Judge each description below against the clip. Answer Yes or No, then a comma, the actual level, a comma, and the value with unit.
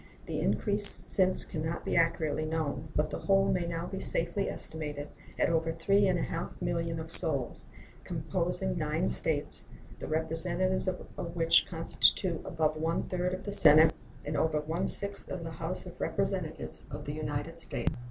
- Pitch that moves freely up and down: No, narrow, 2.6 semitones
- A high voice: No, medium, 165 Hz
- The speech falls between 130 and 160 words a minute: No, average, 170 wpm